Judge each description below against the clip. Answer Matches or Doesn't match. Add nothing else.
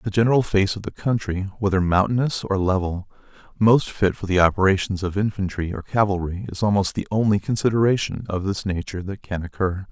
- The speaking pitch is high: Doesn't match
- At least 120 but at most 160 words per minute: Doesn't match